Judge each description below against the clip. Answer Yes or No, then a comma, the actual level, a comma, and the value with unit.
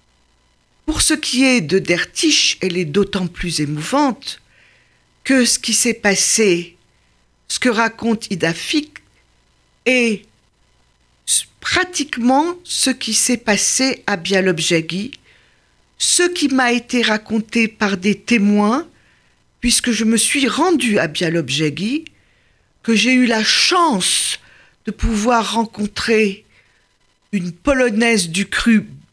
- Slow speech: Yes, slow, 115 wpm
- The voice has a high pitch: Yes, high, 225 Hz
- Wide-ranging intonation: No, average, 4.3 semitones